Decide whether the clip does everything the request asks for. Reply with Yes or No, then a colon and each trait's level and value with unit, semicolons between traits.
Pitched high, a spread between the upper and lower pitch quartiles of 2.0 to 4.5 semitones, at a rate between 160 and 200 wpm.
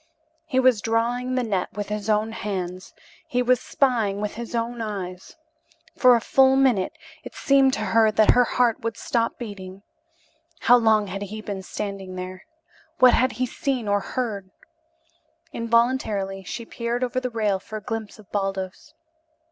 Yes: high, 220 Hz; average, 3.6 semitones; average, 165 wpm